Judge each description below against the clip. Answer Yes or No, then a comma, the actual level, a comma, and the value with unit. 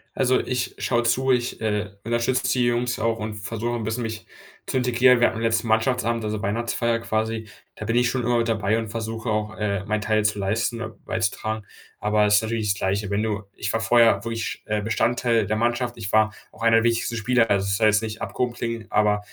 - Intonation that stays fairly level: Yes, narrow, 1.8 semitones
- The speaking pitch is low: Yes, low, 115 Hz